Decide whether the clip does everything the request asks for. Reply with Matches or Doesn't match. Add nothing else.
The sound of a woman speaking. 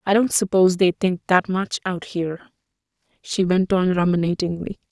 Matches